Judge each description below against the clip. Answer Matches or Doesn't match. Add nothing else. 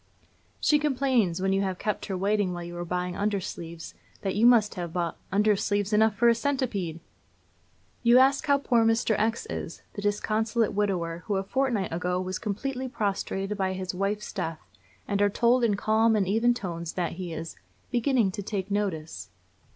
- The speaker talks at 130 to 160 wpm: Doesn't match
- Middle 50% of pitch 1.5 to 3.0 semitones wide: Doesn't match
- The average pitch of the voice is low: Doesn't match